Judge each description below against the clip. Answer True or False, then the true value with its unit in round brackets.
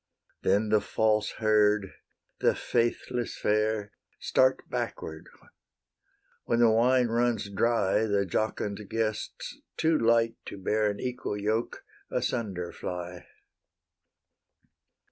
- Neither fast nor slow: False (105 wpm)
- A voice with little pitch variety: True (2.3 semitones)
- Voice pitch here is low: True (110 Hz)